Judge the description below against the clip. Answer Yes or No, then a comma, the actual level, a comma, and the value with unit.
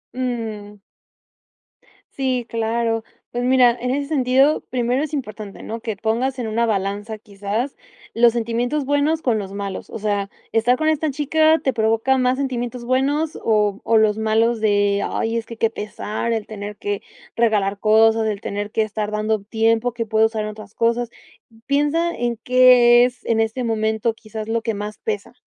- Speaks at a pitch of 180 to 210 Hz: No, high, 230 Hz